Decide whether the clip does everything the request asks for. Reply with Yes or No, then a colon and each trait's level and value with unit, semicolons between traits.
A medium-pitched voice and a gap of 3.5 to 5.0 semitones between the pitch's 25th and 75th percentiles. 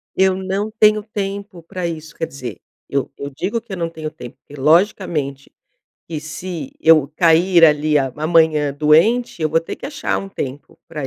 Yes: medium, 165 Hz; average, 4.2 semitones